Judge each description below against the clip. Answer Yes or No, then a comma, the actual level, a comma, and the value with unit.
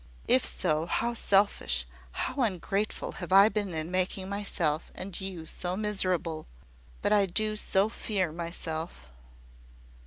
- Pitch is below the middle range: No, medium, 185 Hz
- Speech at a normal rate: No, slow, 130 wpm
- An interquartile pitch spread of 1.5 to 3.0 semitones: No, average, 3.7 semitones